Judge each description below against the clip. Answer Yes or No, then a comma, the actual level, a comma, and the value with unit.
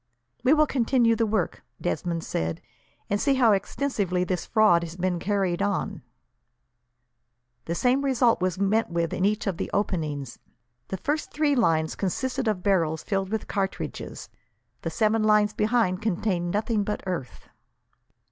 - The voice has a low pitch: No, high, 200 Hz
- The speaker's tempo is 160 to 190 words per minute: No, average, 150 wpm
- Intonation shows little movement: No, average, 4.3 semitones